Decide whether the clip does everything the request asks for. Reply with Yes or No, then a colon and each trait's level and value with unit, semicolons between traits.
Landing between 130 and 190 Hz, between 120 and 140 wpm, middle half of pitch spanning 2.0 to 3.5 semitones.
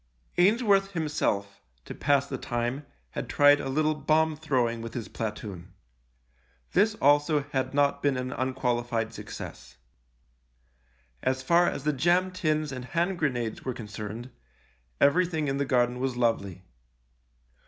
No: low, 135 Hz; slow, 135 wpm; average, 4.3 semitones